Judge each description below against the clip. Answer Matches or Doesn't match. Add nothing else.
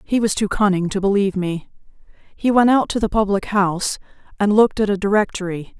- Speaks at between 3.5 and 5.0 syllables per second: Doesn't match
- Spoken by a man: Doesn't match